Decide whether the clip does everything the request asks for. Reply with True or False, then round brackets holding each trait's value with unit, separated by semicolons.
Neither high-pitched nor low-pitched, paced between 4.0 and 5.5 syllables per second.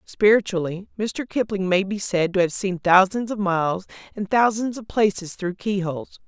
False (195 Hz; 4.9 syllables/s)